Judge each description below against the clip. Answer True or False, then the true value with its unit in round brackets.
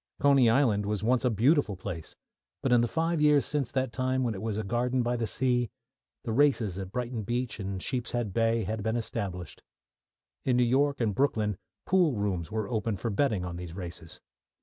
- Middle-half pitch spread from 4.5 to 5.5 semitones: False (4.0 semitones)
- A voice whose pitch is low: True (115 Hz)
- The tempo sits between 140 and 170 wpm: False (195 wpm)